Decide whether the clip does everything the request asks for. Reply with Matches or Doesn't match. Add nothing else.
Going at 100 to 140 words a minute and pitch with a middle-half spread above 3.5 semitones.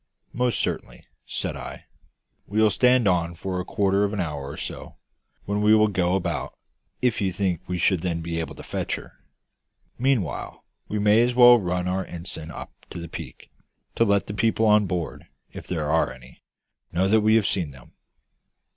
Doesn't match